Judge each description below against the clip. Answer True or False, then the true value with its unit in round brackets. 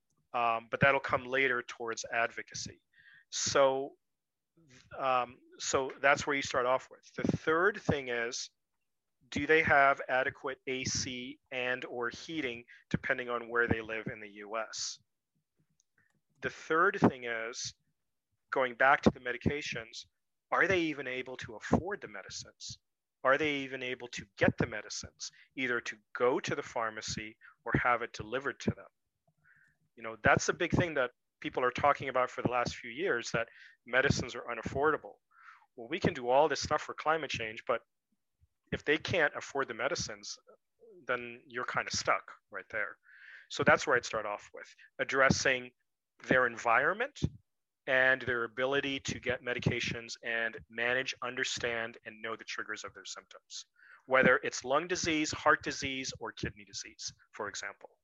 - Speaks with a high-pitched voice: False (130 Hz)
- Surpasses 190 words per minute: False (160 wpm)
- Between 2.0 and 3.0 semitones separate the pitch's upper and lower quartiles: True (2.5 semitones)